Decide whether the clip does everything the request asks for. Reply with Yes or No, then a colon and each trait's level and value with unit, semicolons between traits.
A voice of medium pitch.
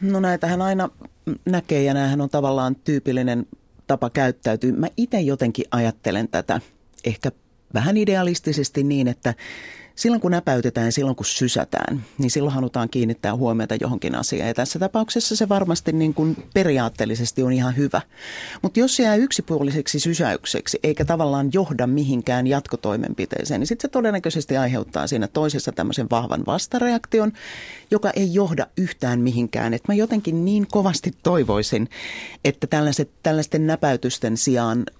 Yes: medium, 145 Hz